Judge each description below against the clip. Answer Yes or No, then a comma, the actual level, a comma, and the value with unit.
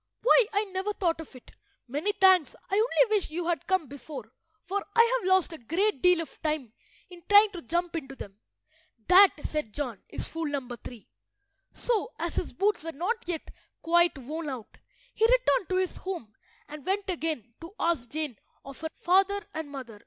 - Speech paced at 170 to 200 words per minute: Yes, average, 190 wpm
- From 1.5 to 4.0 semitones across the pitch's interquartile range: No, average, 5.3 semitones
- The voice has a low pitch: No, very high, 335 Hz